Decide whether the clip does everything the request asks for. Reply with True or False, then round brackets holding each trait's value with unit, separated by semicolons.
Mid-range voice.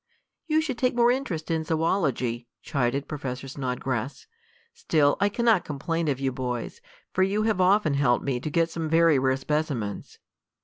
True (155 Hz)